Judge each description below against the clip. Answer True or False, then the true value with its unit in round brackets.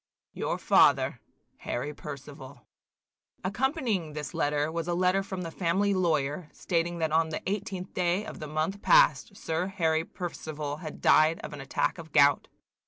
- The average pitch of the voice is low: False (165 Hz)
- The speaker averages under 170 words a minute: True (160 wpm)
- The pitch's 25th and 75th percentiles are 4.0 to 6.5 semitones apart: False (3.6 semitones)